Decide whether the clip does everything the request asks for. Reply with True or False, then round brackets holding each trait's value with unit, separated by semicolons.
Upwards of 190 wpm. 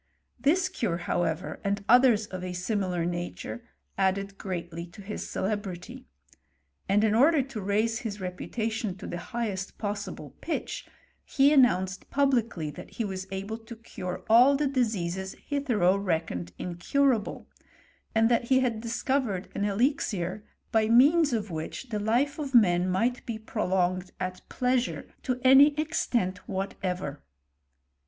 False (140 wpm)